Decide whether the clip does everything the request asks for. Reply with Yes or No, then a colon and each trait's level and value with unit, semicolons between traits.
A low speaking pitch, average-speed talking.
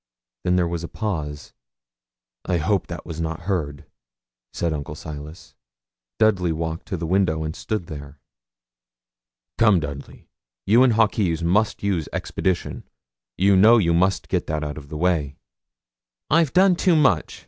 Yes: very low, 85 Hz; average, 150 wpm